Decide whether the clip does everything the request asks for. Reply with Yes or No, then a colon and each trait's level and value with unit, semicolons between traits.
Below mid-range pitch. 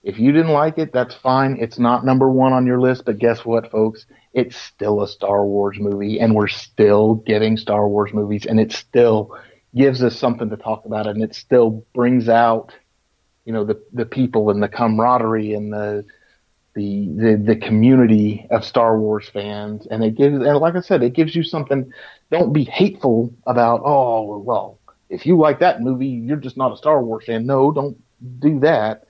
Yes: low, 115 Hz